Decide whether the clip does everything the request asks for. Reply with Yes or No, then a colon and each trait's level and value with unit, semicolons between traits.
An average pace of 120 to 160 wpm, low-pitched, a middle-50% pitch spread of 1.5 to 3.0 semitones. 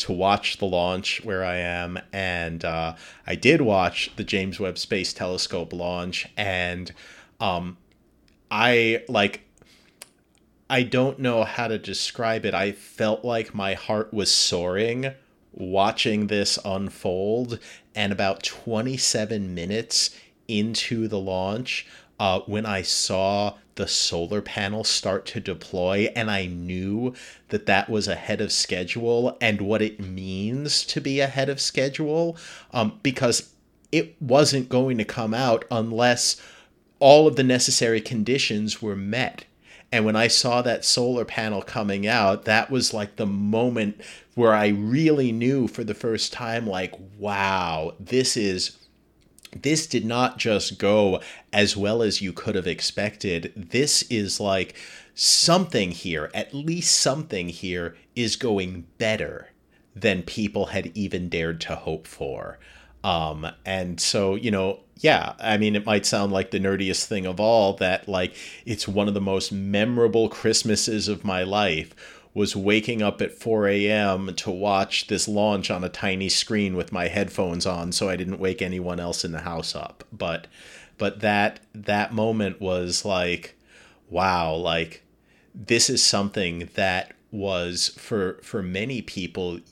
No: average, 150 wpm; low, 105 Hz; average, 3.4 semitones